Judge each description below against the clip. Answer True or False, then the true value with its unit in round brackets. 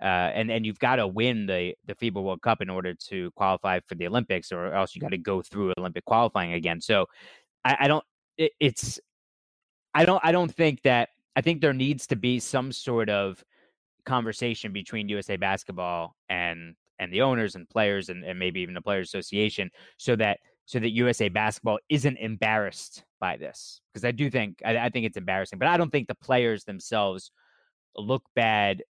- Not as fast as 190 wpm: False (195 wpm)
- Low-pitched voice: True (110 Hz)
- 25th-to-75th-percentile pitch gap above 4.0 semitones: True (5.4 semitones)